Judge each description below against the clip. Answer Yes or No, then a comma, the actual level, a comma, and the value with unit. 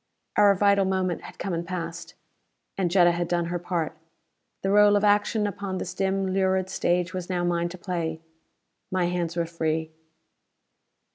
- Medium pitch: Yes, medium, 180 Hz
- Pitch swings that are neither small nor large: No, narrow, 2.0 semitones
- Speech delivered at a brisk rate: No, average, 165 wpm